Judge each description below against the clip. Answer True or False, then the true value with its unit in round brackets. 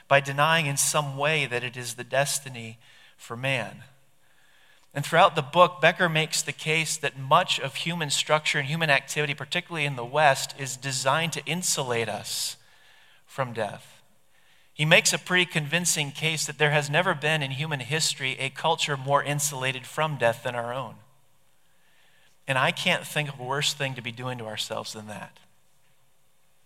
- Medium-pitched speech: True (145 Hz)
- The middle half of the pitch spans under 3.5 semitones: True (3.0 semitones)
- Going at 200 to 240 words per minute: False (175 wpm)